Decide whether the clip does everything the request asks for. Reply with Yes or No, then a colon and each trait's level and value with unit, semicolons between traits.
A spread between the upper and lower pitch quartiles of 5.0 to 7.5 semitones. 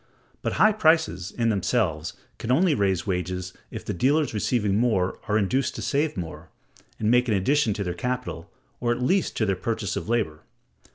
Yes: wide, 5.4 semitones